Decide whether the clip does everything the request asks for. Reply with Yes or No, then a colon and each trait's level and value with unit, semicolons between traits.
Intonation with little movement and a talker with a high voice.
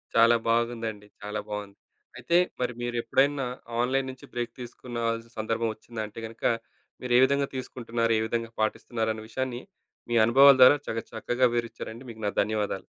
No: narrow, 2.0 semitones; low, 115 Hz